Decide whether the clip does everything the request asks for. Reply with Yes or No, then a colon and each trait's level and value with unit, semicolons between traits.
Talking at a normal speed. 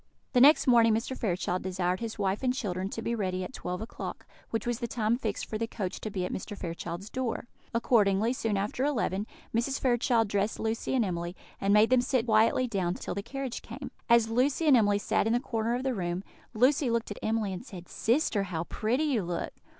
No: fast, 220 wpm